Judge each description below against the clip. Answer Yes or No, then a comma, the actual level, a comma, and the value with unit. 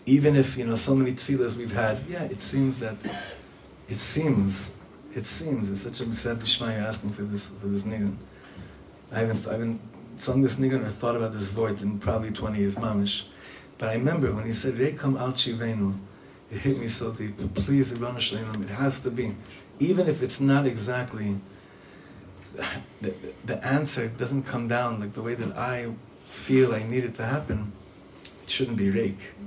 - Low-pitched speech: Yes, low, 115 Hz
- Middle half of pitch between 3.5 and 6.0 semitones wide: Yes, average, 4.0 semitones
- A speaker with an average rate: Yes, average, 185 wpm